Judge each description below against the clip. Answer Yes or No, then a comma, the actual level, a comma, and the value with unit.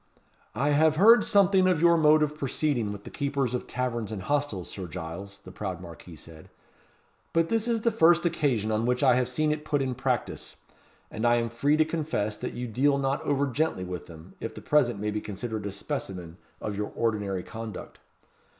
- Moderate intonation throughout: No, wide, 6.7 semitones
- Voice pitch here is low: Yes, low, 125 Hz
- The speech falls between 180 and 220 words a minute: Yes, fast, 205 wpm